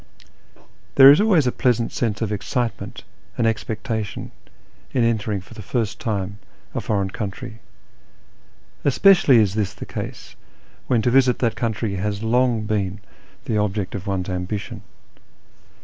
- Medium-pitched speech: No, low, 110 Hz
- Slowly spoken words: No, average, 145 wpm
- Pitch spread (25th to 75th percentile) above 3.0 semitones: Yes, average, 3.4 semitones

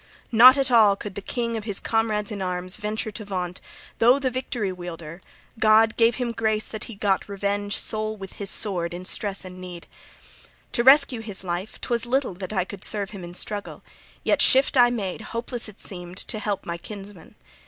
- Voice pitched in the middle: No, high, 210 Hz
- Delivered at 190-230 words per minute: Yes, average, 195 wpm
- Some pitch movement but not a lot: Yes, average, 3.3 semitones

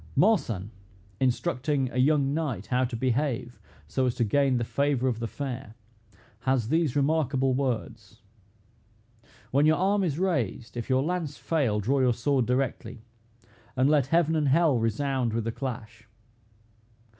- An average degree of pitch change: Yes, average, 3.6 semitones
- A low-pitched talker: Yes, low, 130 Hz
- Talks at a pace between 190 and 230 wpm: No, average, 150 wpm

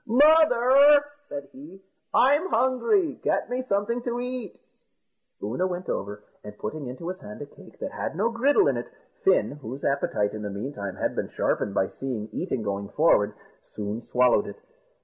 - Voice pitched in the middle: Yes, medium, 175 Hz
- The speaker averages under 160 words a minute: No, average, 170 wpm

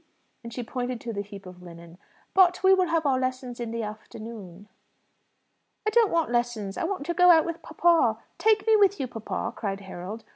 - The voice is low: No, high, 245 Hz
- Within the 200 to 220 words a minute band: Yes, fast, 205 wpm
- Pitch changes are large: Yes, wide, 8.4 semitones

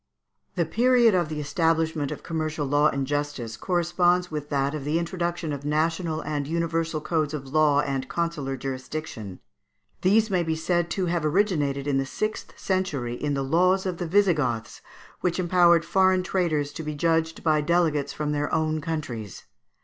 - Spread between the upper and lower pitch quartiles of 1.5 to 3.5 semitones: Yes, average, 3.1 semitones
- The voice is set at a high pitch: No, medium, 155 Hz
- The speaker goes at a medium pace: Yes, average, 170 wpm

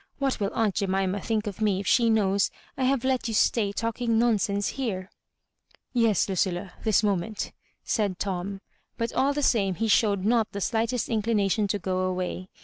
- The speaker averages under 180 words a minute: No, average, 190 wpm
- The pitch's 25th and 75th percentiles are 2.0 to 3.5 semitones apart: Yes, average, 2.9 semitones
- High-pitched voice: Yes, high, 210 Hz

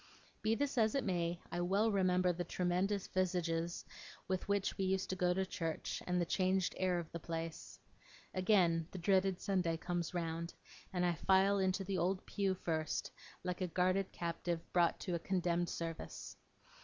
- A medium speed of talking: Yes, average, 175 wpm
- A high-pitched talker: No, medium, 180 Hz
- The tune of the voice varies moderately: No, narrow, 1.9 semitones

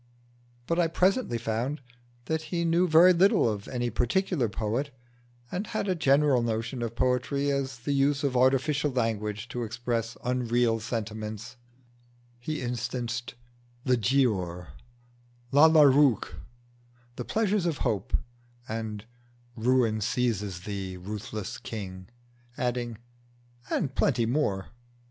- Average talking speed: No, slow, 120 wpm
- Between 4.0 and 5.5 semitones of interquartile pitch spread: Yes, average, 4.4 semitones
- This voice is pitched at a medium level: No, low, 120 Hz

